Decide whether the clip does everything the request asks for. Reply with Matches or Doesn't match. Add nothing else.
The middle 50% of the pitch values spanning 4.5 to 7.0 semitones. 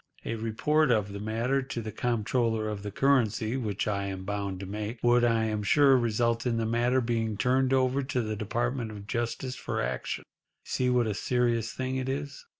Doesn't match